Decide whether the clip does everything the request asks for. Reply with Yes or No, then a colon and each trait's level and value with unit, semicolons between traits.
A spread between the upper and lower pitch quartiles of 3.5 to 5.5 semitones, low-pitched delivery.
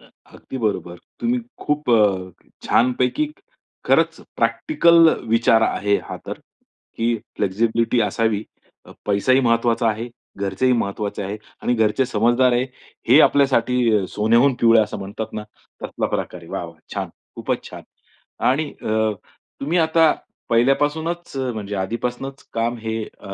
Yes: average, 3.9 semitones; low, 115 Hz